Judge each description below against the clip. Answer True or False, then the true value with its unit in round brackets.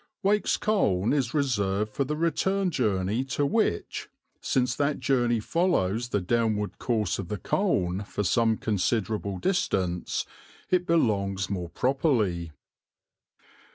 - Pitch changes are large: True (6.6 semitones)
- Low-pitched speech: True (115 Hz)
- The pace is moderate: False (120 wpm)